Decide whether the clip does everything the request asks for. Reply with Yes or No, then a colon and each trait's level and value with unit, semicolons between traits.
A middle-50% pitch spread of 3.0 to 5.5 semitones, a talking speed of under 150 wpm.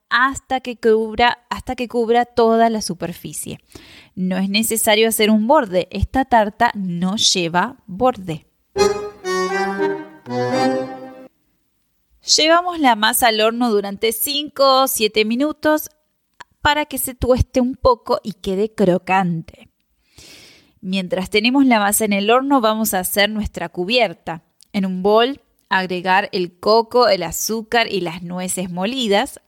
Yes: average, 4.9 semitones; average, 130 wpm